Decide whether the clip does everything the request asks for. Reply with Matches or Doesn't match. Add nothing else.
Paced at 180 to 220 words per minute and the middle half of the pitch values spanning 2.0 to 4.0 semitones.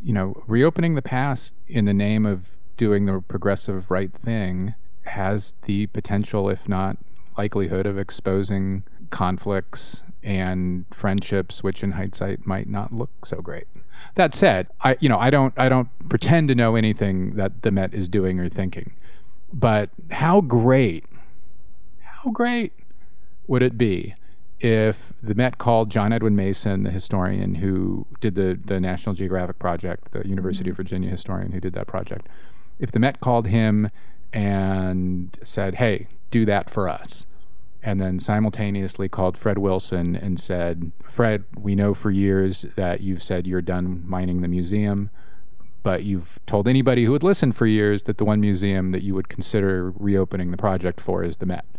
Doesn't match